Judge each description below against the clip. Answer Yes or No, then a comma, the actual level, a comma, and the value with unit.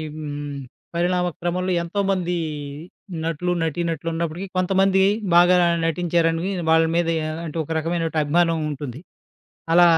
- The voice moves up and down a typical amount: No, narrow, 1.7 semitones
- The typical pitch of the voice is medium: Yes, medium, 170 Hz